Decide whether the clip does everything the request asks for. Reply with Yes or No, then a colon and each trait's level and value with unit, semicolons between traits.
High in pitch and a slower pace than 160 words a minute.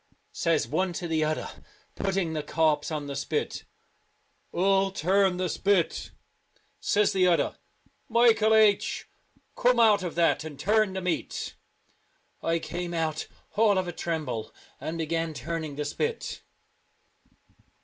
No: medium, 175 Hz; average, 150 wpm